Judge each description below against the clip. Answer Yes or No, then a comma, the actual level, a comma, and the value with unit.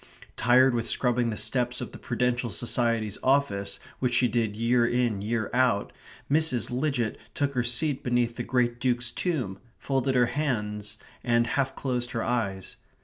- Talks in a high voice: No, low, 120 Hz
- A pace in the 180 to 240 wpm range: No, average, 160 wpm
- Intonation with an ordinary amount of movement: No, narrow, 1.8 semitones